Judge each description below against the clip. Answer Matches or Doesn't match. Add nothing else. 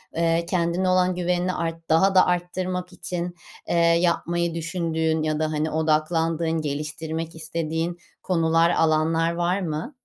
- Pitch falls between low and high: Matches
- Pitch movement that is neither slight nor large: Doesn't match